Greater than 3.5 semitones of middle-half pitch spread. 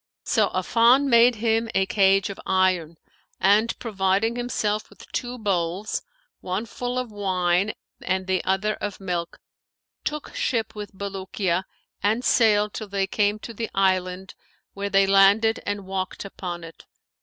No: average, 2.8 semitones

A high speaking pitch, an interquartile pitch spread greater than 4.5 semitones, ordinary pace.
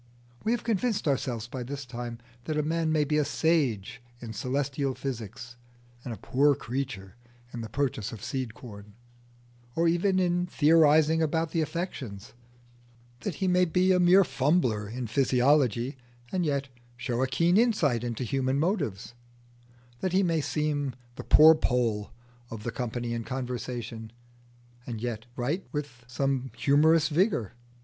No: low, 135 Hz; average, 5.2 semitones; average, 155 wpm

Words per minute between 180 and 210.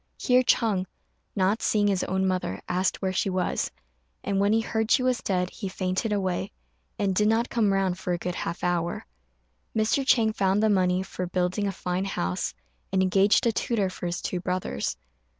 Yes: average, 190 wpm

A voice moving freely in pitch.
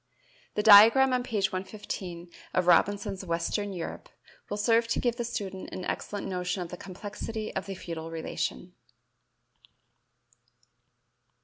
No: average, 3.4 semitones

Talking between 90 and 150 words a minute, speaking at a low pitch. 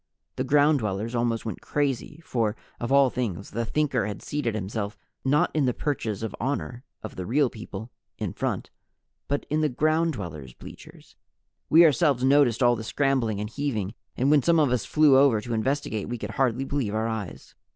No: average, 190 wpm; low, 125 Hz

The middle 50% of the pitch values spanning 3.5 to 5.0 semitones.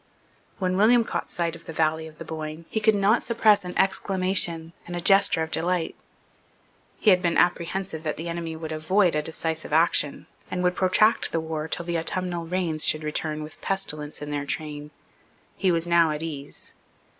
No: average, 2.7 semitones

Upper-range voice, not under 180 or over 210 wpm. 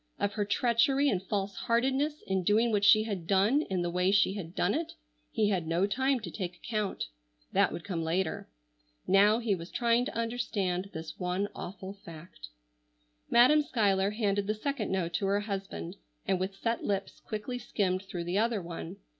Yes: high, 200 Hz; average, 185 wpm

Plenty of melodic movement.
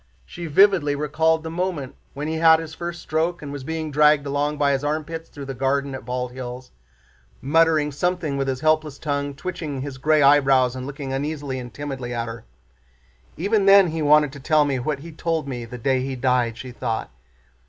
No: average, 3.1 semitones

